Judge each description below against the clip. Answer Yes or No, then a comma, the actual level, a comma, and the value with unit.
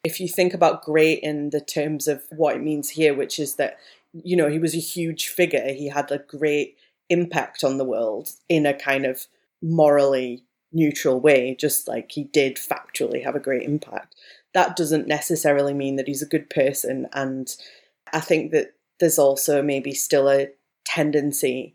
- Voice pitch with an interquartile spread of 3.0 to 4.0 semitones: No, narrow, 2.5 semitones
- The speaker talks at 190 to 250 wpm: No, average, 180 wpm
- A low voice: No, medium, 150 Hz